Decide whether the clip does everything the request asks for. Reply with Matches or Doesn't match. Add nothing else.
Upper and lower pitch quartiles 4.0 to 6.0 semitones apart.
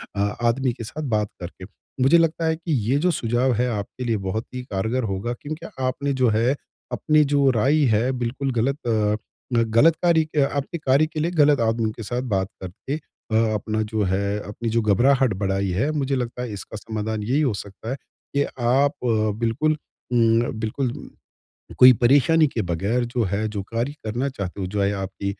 Matches